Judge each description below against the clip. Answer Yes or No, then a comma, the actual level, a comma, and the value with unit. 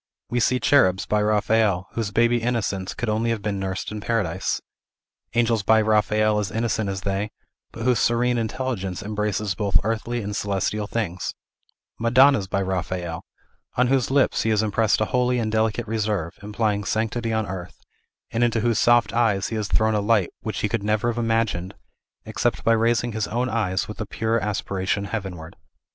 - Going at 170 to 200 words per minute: Yes, average, 180 wpm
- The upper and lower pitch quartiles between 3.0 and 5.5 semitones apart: No, narrow, 2.5 semitones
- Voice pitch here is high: No, low, 110 Hz